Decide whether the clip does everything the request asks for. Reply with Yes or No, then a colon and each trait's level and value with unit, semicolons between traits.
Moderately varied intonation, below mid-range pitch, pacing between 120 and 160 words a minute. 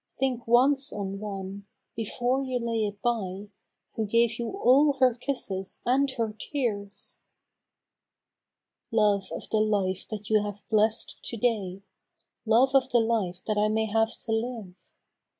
No: average, 3.2 semitones; high, 220 Hz; average, 150 wpm